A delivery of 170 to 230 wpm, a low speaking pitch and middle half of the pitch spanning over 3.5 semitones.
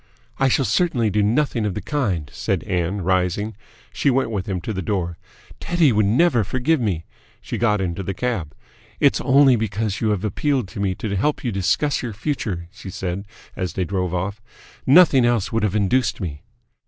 Yes: average, 190 wpm; low, 105 Hz; average, 4.9 semitones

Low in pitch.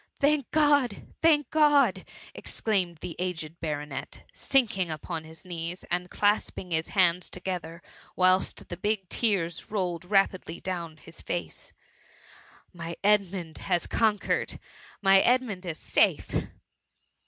No: medium, 185 Hz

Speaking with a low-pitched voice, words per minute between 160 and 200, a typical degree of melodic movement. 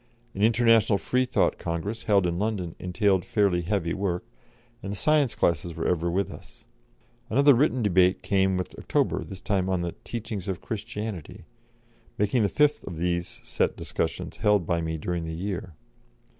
Yes: very low, 95 Hz; average, 165 wpm; average, 3.8 semitones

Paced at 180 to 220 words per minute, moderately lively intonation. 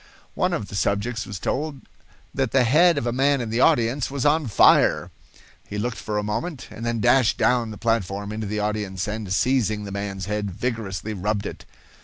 Yes: average, 200 wpm; average, 3.5 semitones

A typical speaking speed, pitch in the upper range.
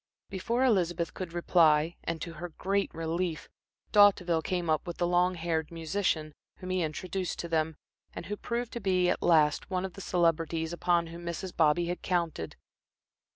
No: average, 175 wpm; medium, 175 Hz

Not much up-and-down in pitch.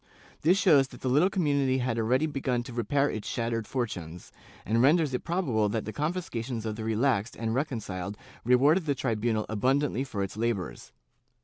No: average, 4.4 semitones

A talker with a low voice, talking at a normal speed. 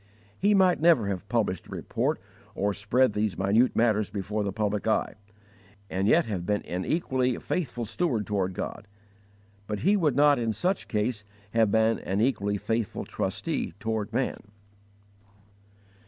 Yes: low, 110 Hz; average, 155 wpm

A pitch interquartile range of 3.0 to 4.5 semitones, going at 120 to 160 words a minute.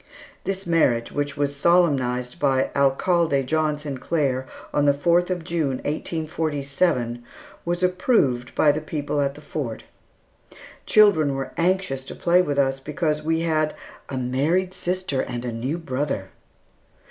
Yes: average, 4.0 semitones; average, 140 wpm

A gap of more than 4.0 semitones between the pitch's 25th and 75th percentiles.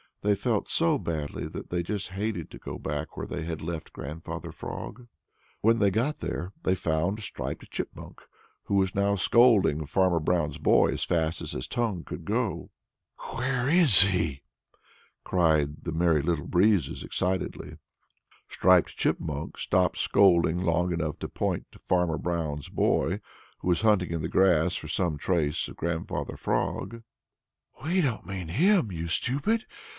Yes: average, 4.4 semitones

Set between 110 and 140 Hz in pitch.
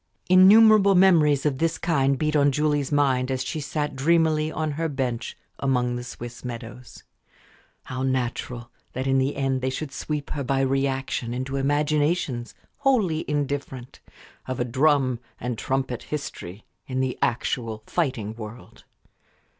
Yes: low, 135 Hz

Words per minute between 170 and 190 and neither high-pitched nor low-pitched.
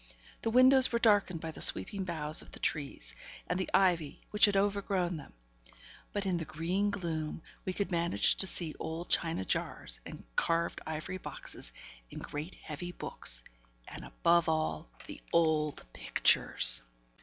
No: average, 155 wpm; medium, 170 Hz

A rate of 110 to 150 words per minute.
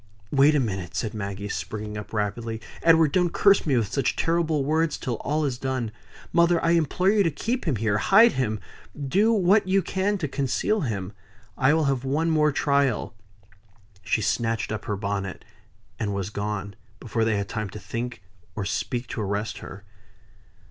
No: average, 180 wpm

